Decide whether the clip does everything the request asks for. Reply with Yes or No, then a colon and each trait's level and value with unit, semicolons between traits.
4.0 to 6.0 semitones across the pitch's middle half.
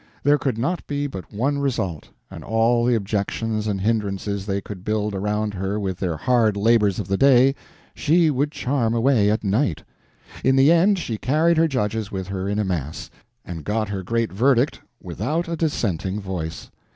Yes: wide, 5.4 semitones